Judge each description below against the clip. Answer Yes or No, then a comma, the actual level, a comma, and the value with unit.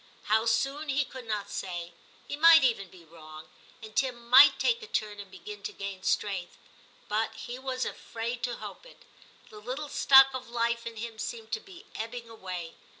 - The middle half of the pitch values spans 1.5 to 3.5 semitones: No, average, 4.4 semitones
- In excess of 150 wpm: Yes, average, 190 wpm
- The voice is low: No, high, 235 Hz